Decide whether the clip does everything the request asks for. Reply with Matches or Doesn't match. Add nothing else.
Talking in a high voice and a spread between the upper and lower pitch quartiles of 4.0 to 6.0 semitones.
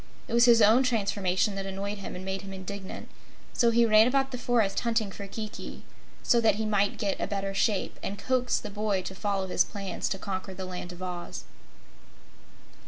Doesn't match